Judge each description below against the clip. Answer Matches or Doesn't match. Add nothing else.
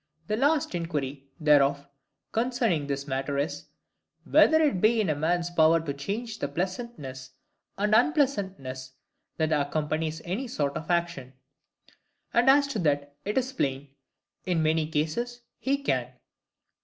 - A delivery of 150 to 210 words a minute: Doesn't match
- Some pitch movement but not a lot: Doesn't match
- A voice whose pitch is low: Doesn't match